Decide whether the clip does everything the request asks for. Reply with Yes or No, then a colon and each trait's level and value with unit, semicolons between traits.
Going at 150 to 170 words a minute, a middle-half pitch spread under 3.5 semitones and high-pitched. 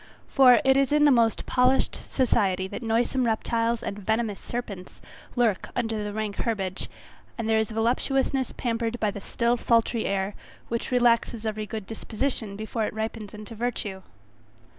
Yes: average, 160 wpm; narrow, 2.4 semitones; high, 225 Hz